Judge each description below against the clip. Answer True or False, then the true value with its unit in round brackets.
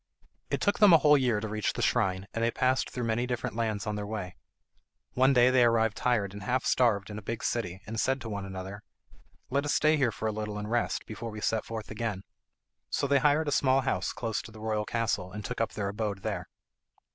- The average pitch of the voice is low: True (115 Hz)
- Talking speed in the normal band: False (240 wpm)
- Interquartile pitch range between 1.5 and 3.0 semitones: False (3.4 semitones)